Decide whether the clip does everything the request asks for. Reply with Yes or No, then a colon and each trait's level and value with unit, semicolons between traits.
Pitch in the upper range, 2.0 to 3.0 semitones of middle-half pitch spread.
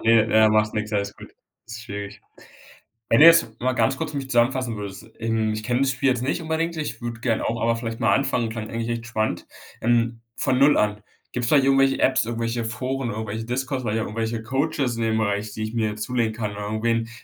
No: low, 115 Hz; average, 2.7 semitones